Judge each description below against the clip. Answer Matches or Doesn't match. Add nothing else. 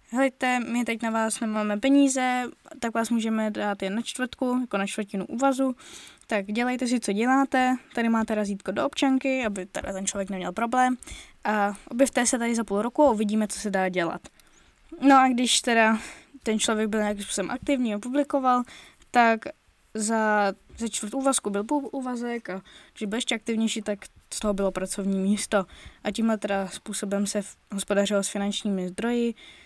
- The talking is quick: Matches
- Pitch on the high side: Matches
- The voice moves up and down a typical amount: Matches